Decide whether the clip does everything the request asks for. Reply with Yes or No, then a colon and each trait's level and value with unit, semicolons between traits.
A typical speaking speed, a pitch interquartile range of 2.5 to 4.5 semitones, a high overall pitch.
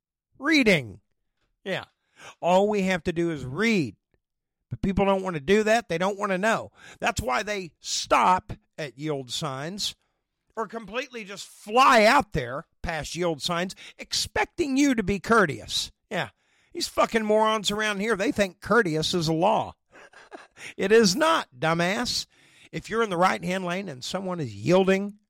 No: average, 165 wpm; average, 4.9 semitones; high, 195 Hz